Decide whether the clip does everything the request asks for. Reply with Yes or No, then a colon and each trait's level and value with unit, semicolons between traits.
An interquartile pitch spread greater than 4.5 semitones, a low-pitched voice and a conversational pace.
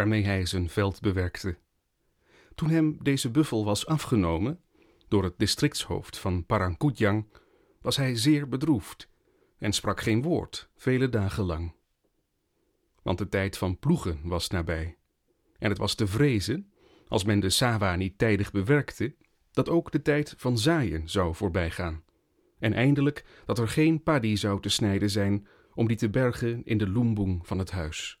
Yes: wide, 5.5 semitones; low, 105 Hz; average, 155 wpm